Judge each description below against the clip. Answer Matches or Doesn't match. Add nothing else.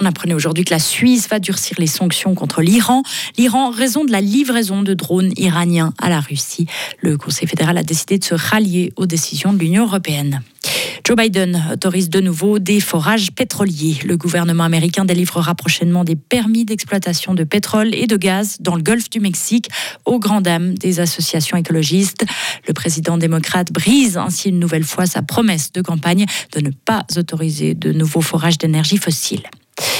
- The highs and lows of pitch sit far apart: Doesn't match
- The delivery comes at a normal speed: Matches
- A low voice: Doesn't match